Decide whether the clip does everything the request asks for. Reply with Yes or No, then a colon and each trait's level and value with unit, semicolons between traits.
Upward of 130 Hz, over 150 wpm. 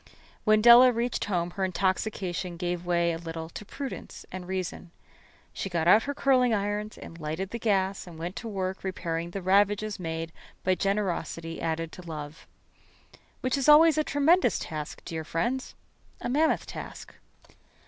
Yes: high, 190 Hz; average, 160 wpm